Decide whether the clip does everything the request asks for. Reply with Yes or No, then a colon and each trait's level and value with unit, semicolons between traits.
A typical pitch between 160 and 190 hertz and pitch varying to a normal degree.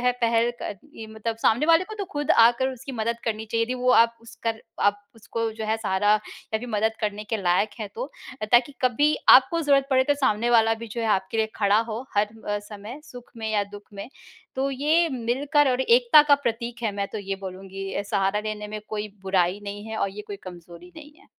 No: high, 225 Hz; average, 3.5 semitones